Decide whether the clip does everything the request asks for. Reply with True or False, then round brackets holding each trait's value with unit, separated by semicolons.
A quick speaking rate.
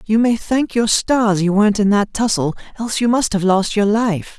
True (230 wpm)